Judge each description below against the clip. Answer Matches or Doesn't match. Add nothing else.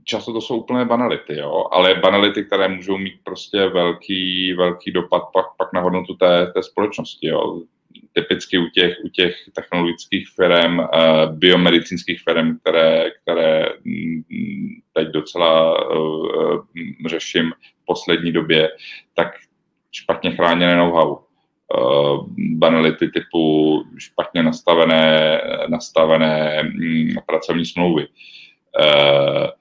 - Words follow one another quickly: Doesn't match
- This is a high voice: Doesn't match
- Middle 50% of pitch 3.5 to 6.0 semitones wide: Doesn't match